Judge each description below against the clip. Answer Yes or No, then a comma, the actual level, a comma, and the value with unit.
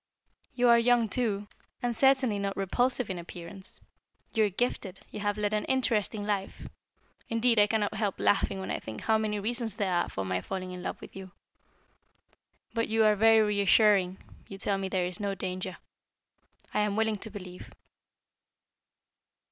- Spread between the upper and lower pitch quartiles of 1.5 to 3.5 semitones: Yes, average, 2.7 semitones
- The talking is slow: No, average, 170 wpm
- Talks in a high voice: Yes, high, 205 Hz